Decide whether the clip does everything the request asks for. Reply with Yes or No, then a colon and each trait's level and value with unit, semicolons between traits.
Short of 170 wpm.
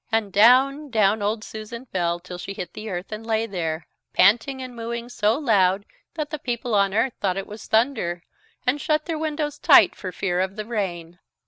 No: average, 200 wpm